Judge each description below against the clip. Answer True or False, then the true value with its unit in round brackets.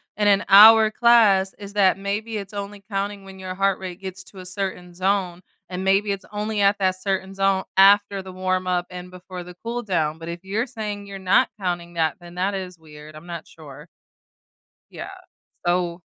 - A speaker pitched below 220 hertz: True (190 Hz)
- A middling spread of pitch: False (2.0 semitones)